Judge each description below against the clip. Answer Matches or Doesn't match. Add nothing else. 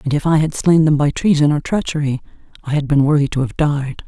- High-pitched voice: Doesn't match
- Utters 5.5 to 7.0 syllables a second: Matches